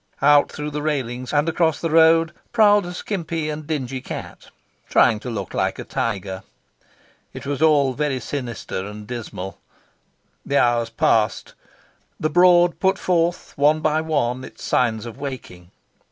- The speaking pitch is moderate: Yes, medium, 145 Hz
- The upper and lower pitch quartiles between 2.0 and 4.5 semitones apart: No, average, 5.1 semitones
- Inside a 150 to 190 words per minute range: Yes, average, 155 wpm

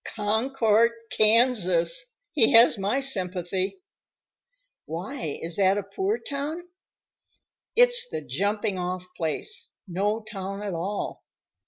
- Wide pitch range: Yes, wide, 6.5 semitones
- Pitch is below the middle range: No, high, 210 Hz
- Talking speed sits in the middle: No, slow, 110 wpm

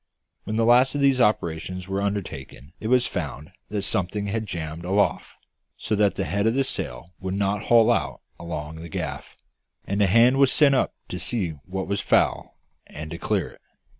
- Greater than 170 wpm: Yes, average, 195 wpm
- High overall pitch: No, low, 100 Hz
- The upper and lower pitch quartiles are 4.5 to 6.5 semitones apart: Yes, average, 4.8 semitones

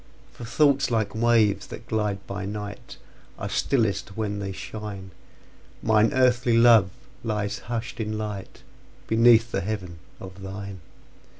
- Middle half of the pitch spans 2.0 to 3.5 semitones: Yes, average, 2.7 semitones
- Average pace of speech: No, slow, 115 wpm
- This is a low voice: Yes, low, 105 Hz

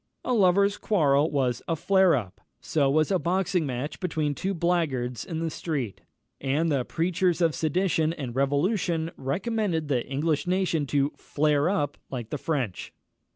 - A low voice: No, medium, 155 Hz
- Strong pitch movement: No, average, 4.4 semitones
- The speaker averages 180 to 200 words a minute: No, average, 155 wpm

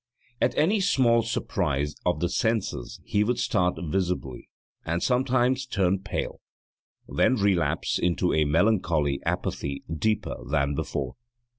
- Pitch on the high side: No, very low, 95 Hz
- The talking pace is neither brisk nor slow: No, slow, 125 wpm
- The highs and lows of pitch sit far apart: Yes, wide, 7.2 semitones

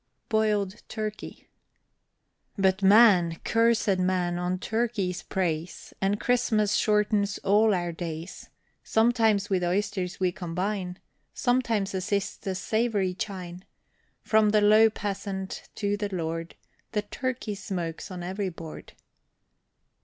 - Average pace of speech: No, slow, 115 wpm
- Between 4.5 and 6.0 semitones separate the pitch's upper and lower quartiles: No, average, 2.9 semitones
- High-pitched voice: Yes, high, 200 Hz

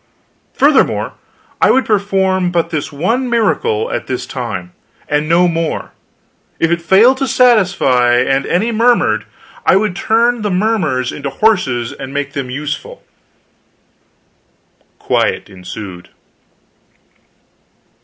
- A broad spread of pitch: Yes, wide, 8.0 semitones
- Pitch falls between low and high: Yes, medium, 170 Hz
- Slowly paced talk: Yes, slow, 115 wpm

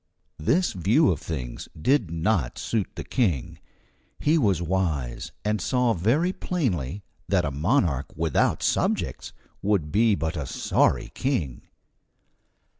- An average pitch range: No, wide, 7.4 semitones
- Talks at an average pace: No, slow, 125 wpm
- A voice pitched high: No, very low, 90 Hz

